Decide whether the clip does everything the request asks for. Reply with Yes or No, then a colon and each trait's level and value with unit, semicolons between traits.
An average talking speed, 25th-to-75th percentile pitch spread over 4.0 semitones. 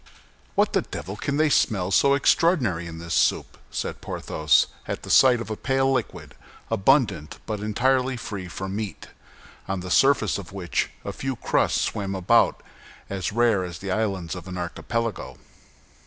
Yes: average, 165 wpm; average, 5.2 semitones